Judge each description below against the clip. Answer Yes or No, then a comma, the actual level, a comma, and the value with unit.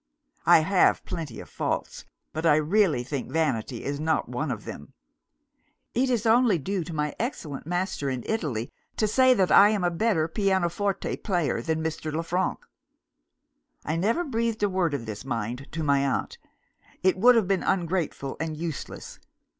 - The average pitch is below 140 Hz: No, medium, 165 Hz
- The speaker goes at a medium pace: Yes, average, 170 wpm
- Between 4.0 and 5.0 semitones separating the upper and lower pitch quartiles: No, wide, 5.6 semitones